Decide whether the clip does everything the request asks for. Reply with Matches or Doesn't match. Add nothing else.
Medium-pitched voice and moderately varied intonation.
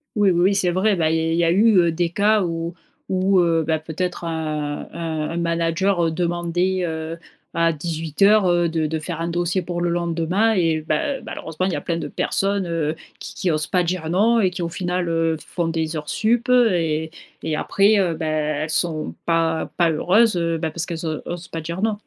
Doesn't match